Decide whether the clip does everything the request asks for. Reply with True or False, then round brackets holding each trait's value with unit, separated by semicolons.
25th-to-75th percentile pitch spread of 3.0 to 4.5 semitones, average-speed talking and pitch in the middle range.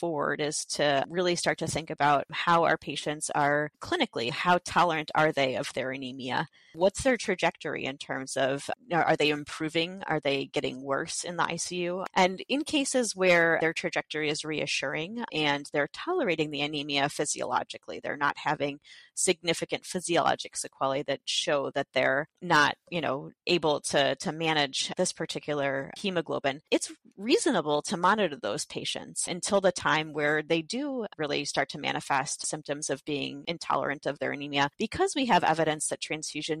True (3.7 semitones; 160 wpm; 155 Hz)